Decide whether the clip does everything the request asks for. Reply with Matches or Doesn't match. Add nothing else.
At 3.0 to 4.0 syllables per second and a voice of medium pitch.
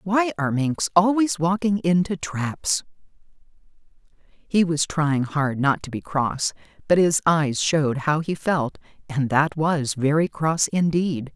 Matches